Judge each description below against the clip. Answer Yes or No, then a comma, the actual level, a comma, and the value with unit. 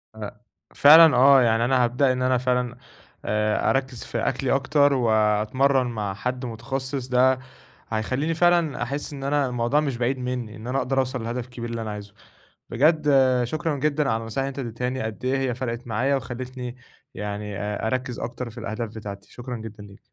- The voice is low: Yes, low, 125 Hz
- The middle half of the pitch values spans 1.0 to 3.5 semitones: Yes, average, 3.0 semitones